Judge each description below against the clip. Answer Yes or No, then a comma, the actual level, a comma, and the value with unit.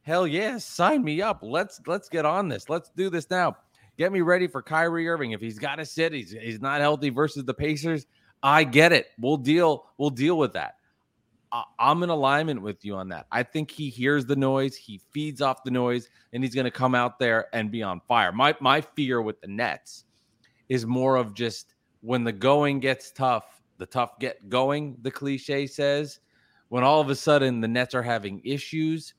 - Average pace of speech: No, fast, 210 wpm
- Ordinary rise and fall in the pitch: Yes, average, 3.7 semitones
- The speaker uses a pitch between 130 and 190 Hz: Yes, low, 135 Hz